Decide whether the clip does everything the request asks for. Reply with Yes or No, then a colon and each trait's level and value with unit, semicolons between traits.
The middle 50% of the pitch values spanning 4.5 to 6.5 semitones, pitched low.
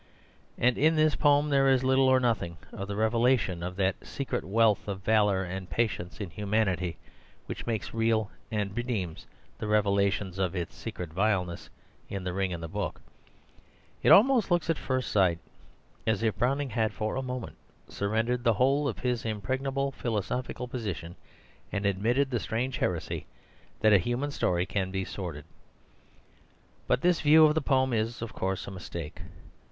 Yes: average, 5.1 semitones; low, 110 Hz